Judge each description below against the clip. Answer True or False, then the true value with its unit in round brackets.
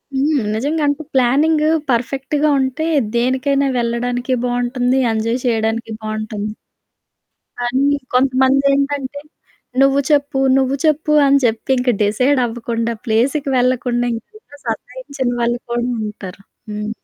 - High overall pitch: True (255 Hz)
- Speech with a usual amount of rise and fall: True (3.0 semitones)